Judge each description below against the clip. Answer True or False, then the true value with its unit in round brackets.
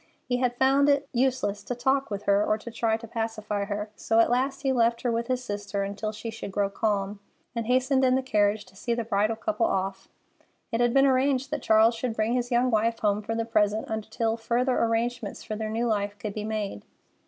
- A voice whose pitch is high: True (225 Hz)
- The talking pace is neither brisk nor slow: False (225 wpm)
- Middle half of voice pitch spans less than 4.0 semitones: True (2.9 semitones)